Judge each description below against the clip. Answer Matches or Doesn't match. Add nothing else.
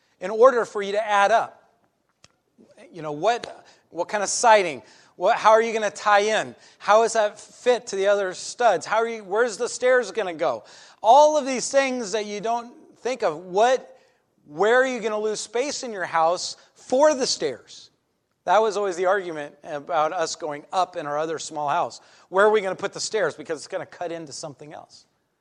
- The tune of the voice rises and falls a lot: Matches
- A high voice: Matches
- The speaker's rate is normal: Doesn't match